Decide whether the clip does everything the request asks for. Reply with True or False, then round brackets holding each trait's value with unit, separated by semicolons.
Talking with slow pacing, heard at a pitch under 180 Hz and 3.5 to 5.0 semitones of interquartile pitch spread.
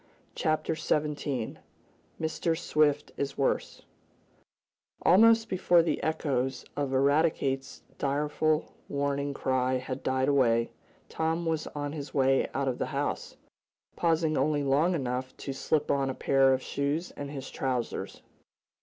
False (130 wpm; 140 Hz; 2.8 semitones)